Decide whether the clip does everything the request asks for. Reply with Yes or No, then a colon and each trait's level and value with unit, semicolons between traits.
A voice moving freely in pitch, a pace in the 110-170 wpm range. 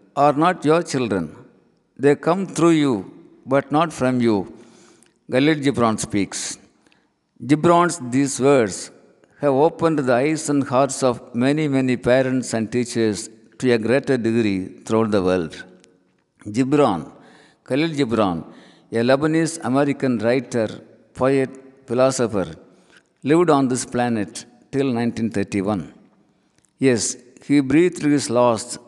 No: average, 4.0 semitones; average, 115 wpm